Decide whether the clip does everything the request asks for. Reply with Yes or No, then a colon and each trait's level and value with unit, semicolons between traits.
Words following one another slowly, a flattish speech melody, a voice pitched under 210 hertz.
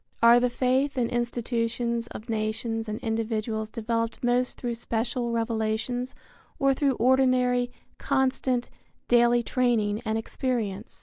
No: slow, 120 wpm; narrow, 1.9 semitones; high, 235 Hz